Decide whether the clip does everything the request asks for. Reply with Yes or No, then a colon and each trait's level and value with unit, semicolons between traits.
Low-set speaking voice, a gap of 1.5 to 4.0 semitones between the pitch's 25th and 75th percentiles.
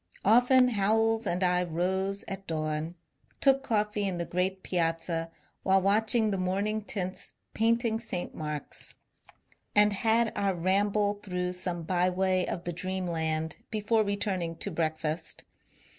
No: high, 190 Hz; average, 3.2 semitones